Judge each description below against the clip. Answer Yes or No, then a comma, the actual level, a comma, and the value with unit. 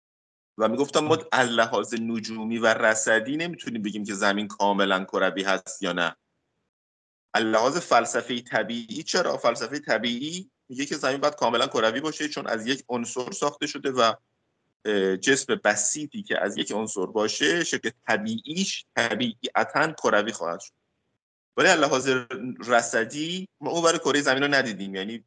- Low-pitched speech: Yes, low, 125 Hz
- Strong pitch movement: Yes, wide, 5.9 semitones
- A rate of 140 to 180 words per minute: Yes, average, 145 wpm